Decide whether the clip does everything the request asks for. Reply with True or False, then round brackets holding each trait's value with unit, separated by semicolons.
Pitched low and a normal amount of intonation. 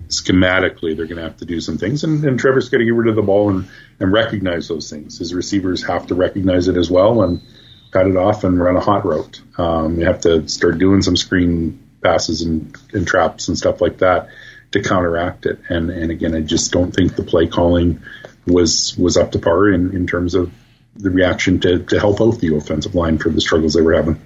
True (90 Hz; 3.2 semitones)